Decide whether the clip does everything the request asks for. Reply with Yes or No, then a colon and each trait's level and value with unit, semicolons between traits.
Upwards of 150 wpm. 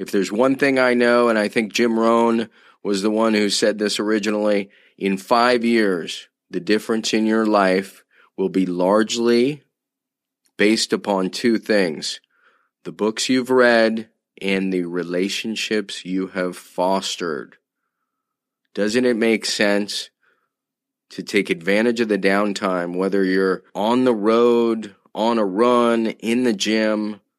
No: average, 140 wpm